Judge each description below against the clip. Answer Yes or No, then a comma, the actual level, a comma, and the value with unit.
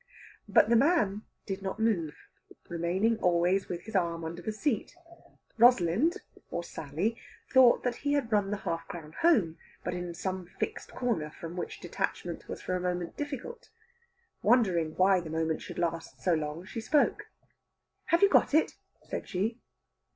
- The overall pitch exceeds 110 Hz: Yes, high, 190 Hz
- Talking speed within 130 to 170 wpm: Yes, average, 160 wpm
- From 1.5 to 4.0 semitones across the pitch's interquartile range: No, average, 5.3 semitones